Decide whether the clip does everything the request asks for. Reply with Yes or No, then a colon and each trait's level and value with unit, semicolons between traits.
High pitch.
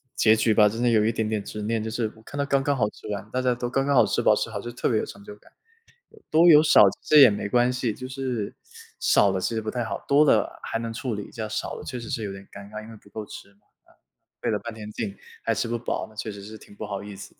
No: low, 110 Hz